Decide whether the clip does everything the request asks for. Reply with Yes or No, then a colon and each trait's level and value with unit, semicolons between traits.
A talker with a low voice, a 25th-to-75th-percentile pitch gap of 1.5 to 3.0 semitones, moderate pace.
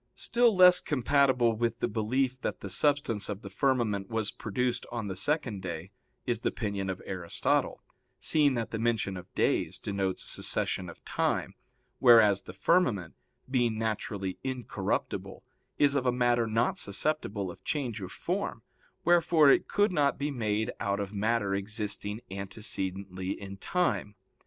No: low, 110 Hz; average, 4.7 semitones; average, 150 wpm